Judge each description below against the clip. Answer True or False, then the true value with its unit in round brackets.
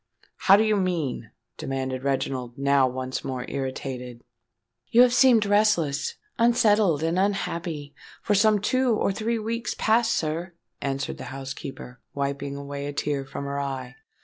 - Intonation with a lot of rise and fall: True (7.6 semitones)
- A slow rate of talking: False (150 wpm)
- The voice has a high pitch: False (145 Hz)